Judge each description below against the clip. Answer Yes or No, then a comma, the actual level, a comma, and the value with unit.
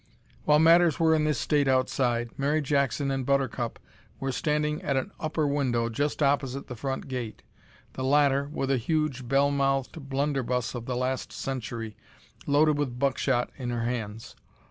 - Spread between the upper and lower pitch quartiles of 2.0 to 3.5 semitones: Yes, average, 2.7 semitones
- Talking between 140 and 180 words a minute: Yes, average, 165 wpm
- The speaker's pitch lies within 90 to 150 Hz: Yes, low, 135 Hz